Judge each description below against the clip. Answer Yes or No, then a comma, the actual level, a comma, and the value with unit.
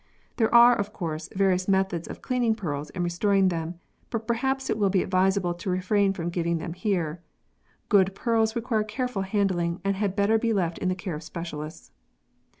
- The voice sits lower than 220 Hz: Yes, high, 190 Hz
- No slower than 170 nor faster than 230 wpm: Yes, average, 185 wpm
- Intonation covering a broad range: No, average, 3.7 semitones